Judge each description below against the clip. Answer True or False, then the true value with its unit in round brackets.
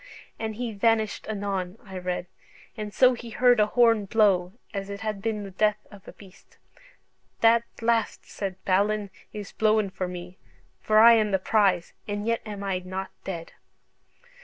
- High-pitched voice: True (205 Hz)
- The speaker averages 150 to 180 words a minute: True (170 wpm)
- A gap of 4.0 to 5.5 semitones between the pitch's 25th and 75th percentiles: False (2.4 semitones)